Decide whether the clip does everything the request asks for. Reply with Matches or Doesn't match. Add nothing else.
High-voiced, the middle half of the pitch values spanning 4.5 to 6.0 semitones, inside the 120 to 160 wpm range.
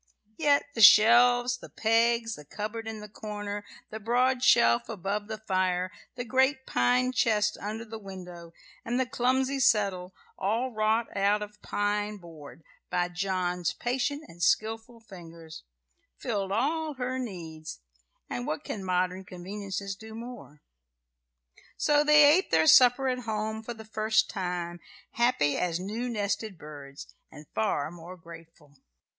Matches